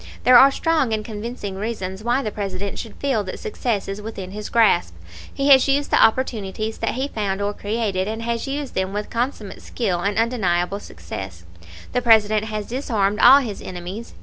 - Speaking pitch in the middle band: No, high, 215 Hz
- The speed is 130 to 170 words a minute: No, average, 190 wpm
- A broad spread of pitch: No, average, 3.5 semitones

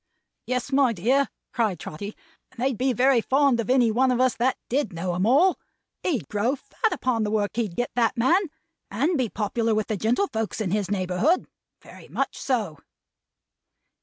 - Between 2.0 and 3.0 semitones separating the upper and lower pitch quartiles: No, average, 4.0 semitones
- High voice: Yes, high, 235 Hz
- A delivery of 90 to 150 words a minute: No, average, 180 wpm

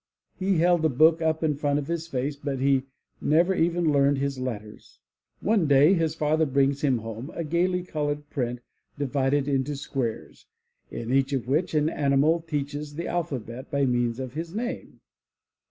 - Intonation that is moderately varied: Yes, average, 3.2 semitones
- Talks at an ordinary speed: Yes, average, 175 wpm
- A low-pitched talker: No, medium, 145 Hz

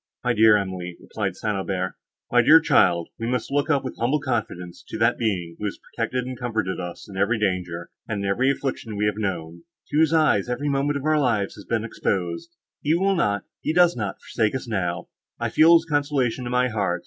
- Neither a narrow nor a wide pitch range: No, wide, 5.9 semitones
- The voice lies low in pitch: Yes, low, 115 Hz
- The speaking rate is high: Yes, fast, 220 wpm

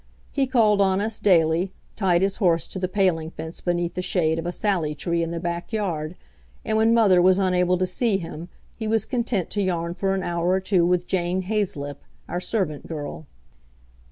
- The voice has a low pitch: No, medium, 180 Hz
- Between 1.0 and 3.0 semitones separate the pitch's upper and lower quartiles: Yes, average, 2.7 semitones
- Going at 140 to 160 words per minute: No, average, 195 wpm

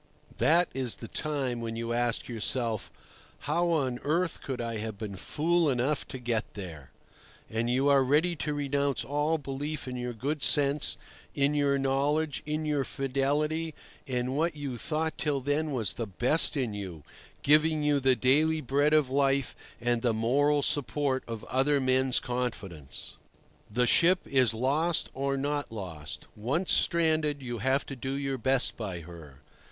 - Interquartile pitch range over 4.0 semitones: No, average, 3.7 semitones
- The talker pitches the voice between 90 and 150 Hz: Yes, low, 135 Hz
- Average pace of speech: Yes, average, 165 wpm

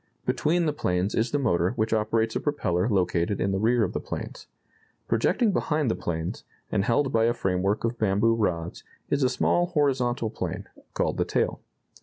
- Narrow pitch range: No, average, 5.1 semitones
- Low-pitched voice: Yes, low, 115 Hz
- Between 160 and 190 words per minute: Yes, average, 185 wpm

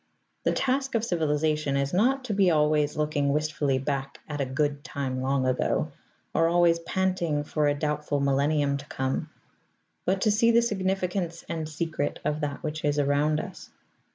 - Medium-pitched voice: Yes, medium, 150 Hz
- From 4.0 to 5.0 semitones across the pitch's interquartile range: No, average, 3.5 semitones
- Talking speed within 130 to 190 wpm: Yes, average, 170 wpm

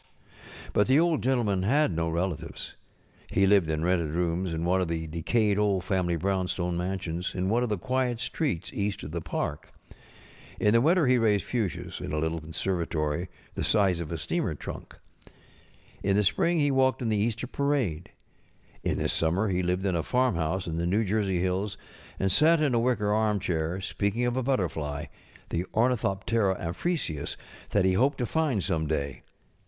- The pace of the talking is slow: No, average, 180 wpm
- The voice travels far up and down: Yes, wide, 5.8 semitones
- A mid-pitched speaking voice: No, very low, 95 Hz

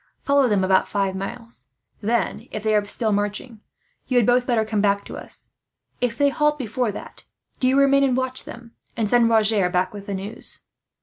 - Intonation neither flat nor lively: Yes, average, 3.5 semitones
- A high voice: Yes, high, 225 Hz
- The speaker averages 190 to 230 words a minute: Yes, average, 200 wpm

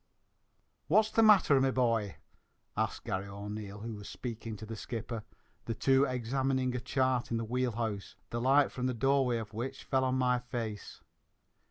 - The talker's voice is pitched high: No, low, 120 Hz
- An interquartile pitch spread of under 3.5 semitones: Yes, average, 2.9 semitones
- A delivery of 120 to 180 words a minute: Yes, average, 175 wpm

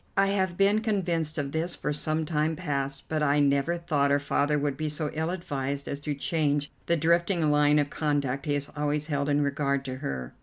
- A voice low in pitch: No, medium, 150 Hz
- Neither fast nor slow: No, fast, 215 wpm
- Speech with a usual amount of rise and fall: No, narrow, 2.3 semitones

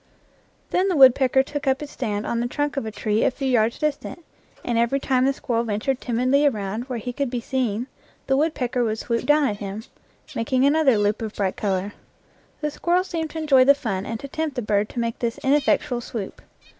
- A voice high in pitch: Yes, very high, 250 Hz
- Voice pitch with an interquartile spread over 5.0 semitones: No, average, 4.1 semitones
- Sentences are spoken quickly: Yes, fast, 215 wpm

